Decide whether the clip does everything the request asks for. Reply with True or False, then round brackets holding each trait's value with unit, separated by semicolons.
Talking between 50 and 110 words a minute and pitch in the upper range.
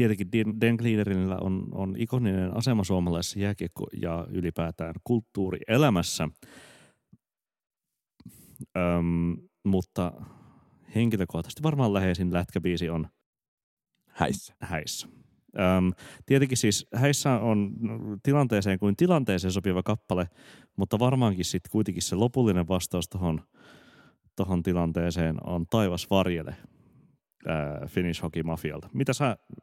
False (95 wpm; 95 Hz)